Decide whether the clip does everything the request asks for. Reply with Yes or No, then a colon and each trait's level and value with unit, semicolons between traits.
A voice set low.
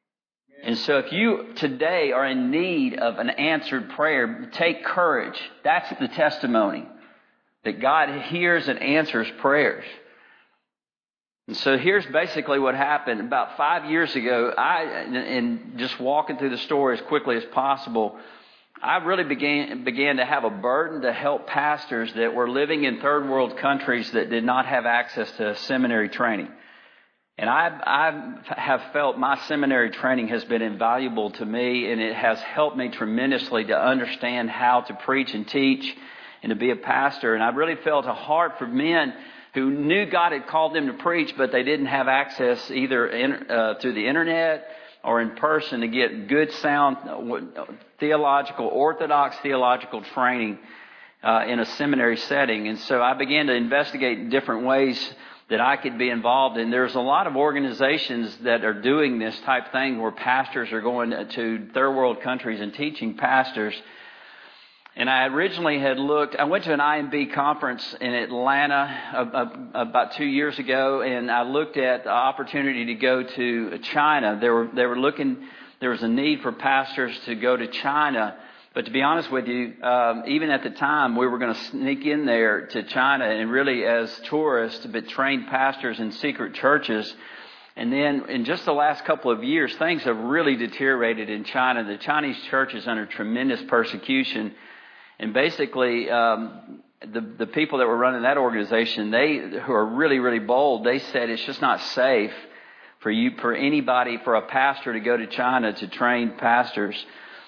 Yes: low, 130 Hz